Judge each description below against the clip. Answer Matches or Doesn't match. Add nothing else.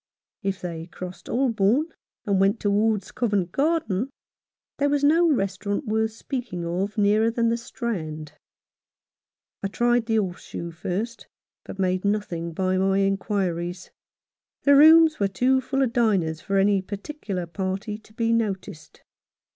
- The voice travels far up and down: Doesn't match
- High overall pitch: Matches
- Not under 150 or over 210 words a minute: Doesn't match